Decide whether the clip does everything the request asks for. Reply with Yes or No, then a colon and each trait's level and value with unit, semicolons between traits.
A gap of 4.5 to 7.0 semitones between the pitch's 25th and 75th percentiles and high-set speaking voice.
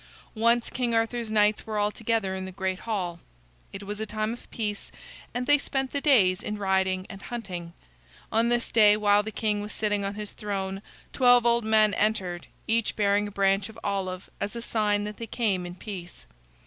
No: narrow, 2.6 semitones; high, 210 Hz